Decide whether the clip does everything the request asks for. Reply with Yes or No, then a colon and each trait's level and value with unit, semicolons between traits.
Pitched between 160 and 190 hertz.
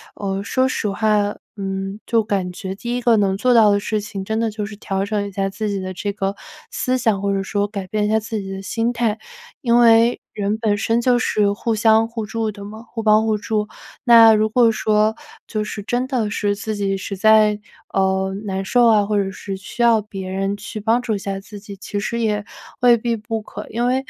No: high, 210 Hz